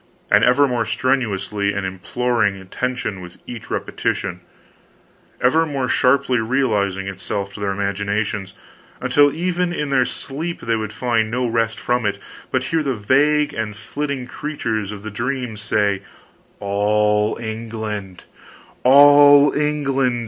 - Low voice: Yes, low, 115 Hz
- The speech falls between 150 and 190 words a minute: No, slow, 135 wpm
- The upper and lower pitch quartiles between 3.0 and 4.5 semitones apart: No, average, 4.9 semitones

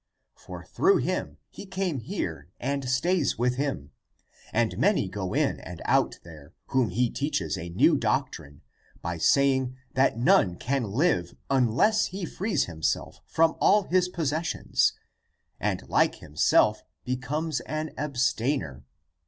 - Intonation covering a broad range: Yes, wide, 8.9 semitones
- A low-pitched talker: Yes, low, 130 Hz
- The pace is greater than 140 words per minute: No, slow, 135 wpm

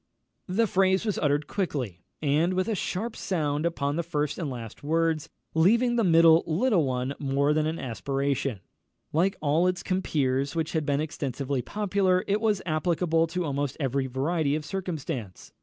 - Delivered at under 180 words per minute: Yes, average, 165 wpm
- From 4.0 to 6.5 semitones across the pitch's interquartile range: Yes, average, 4.5 semitones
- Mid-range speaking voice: Yes, medium, 155 Hz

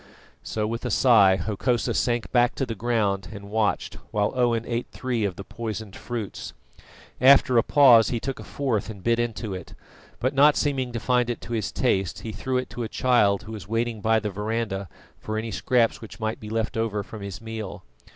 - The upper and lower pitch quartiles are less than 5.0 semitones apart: Yes, narrow, 2.6 semitones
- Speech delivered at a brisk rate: Yes, fast, 210 wpm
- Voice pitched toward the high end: No, low, 115 Hz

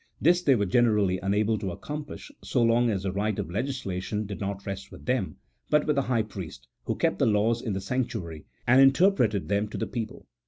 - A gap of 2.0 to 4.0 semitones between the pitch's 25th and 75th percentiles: No, average, 4.4 semitones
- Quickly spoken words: Yes, fast, 220 wpm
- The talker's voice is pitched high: No, low, 110 Hz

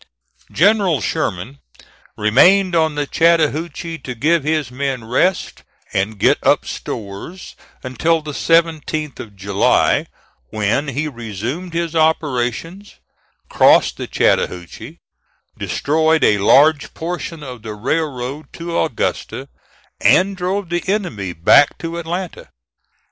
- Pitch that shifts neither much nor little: No, wide, 5.7 semitones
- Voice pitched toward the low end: No, medium, 155 Hz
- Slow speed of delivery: Yes, slow, 115 wpm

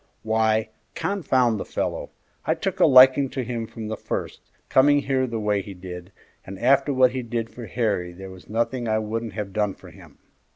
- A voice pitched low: Yes, low, 115 Hz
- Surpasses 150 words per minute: Yes, average, 200 wpm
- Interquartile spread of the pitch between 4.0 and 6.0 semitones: No, average, 3.6 semitones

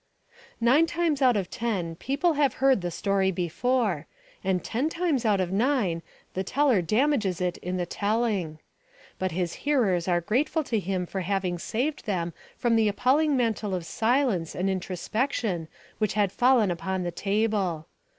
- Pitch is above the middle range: Yes, high, 205 Hz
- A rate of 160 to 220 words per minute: Yes, average, 165 wpm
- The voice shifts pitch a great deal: Yes, wide, 5.8 semitones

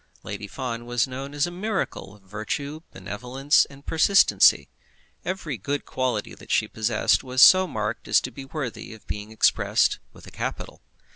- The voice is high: No, low, 130 Hz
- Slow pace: No, average, 165 wpm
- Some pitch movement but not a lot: Yes, average, 5.0 semitones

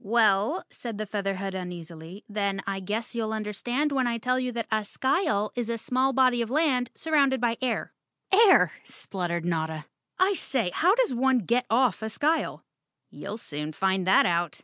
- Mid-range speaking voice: No, high, 225 Hz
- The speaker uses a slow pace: No, average, 180 wpm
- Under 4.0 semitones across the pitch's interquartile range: No, average, 5.0 semitones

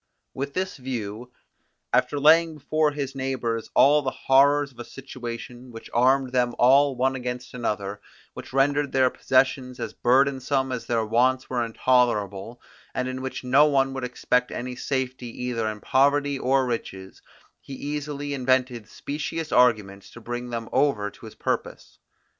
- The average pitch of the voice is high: No, low, 130 Hz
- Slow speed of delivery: No, average, 155 wpm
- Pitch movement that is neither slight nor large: No, narrow, 2.3 semitones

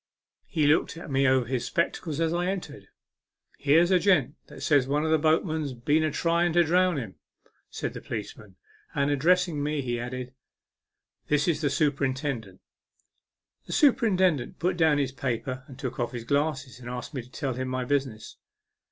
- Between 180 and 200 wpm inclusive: Yes, average, 185 wpm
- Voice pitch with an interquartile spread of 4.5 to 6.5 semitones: No, average, 4.0 semitones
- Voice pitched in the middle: Yes, medium, 145 Hz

